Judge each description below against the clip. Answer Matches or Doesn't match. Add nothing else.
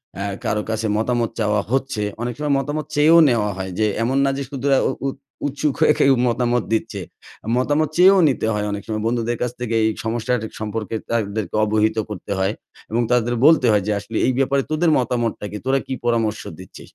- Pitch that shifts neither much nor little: Matches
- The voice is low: Matches